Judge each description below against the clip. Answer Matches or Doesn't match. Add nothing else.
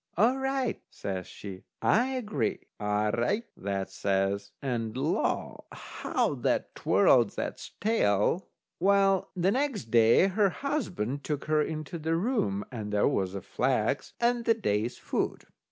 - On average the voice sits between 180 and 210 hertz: Doesn't match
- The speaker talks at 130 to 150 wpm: Matches